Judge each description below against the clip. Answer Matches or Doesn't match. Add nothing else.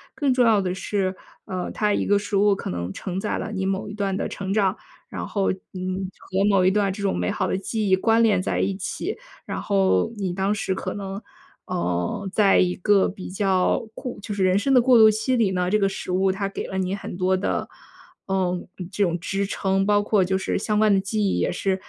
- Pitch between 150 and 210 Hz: Matches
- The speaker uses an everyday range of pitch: Doesn't match